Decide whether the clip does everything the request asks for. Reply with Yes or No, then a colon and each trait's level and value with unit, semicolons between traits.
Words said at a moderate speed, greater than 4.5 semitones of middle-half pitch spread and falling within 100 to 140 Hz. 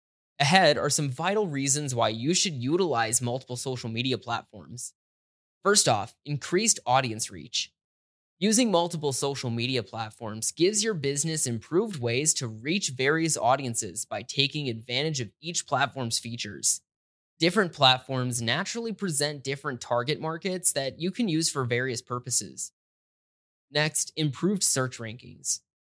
No: slow, 130 wpm; average, 5.2 semitones; low, 135 Hz